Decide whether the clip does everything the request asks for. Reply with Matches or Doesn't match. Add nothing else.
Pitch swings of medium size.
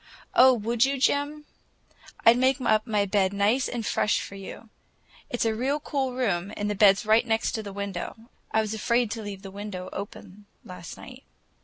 Matches